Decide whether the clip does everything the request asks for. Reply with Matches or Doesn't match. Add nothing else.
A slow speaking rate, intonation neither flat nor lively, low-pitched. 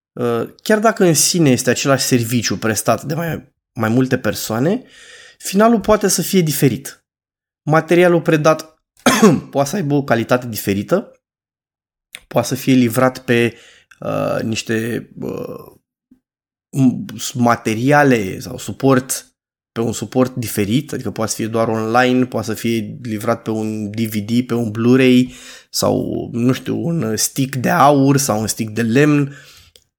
Doesn't match